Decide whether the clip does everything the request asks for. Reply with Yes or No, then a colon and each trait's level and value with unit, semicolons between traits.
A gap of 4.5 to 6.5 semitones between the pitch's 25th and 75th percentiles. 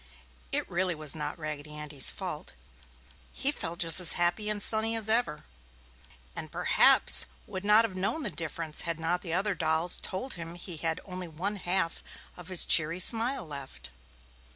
No: average, 3.9 semitones